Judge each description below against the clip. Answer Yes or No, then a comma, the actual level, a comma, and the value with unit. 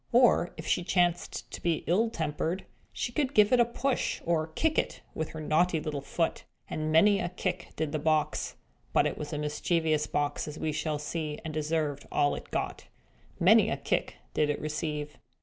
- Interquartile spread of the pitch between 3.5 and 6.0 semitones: No, average, 2.9 semitones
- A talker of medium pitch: Yes, medium, 160 Hz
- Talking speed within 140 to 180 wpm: No, average, 195 wpm